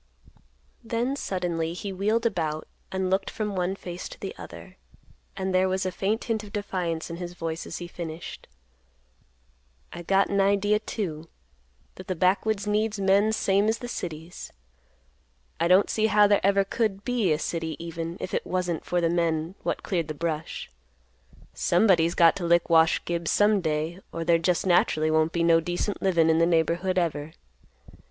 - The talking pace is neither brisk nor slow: Yes, average, 175 wpm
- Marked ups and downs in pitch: No, average, 3.2 semitones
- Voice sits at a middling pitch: Yes, medium, 180 Hz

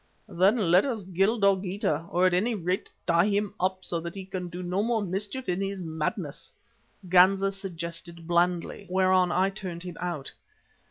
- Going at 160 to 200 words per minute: Yes, average, 170 wpm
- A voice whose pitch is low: No, medium, 185 Hz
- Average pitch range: No, narrow, 2.2 semitones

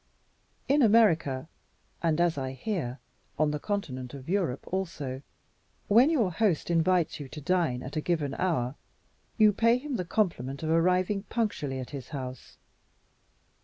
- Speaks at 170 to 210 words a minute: No, average, 150 wpm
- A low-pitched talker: No, medium, 165 Hz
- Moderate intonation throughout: No, wide, 6.7 semitones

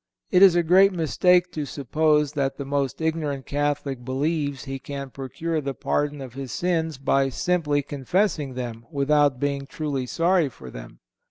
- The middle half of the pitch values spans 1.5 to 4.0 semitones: Yes, average, 3.1 semitones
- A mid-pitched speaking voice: Yes, medium, 145 Hz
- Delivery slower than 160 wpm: No, average, 165 wpm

